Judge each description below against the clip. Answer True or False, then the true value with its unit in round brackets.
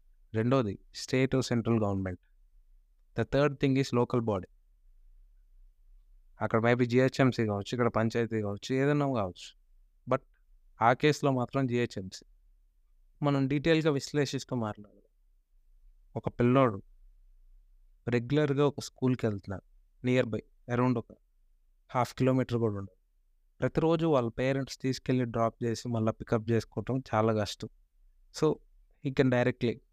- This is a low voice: True (115 Hz)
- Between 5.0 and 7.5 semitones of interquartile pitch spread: True (5.5 semitones)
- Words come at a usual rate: True (110 wpm)